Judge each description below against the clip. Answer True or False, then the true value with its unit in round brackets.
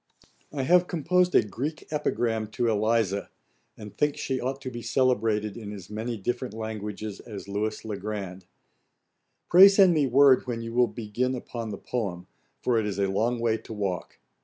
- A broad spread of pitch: False (3.5 semitones)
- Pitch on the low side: True (115 Hz)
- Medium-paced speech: True (180 wpm)